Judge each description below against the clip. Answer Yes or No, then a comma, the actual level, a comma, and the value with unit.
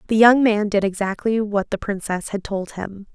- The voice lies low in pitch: No, high, 205 Hz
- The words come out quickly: Yes, fast, 210 wpm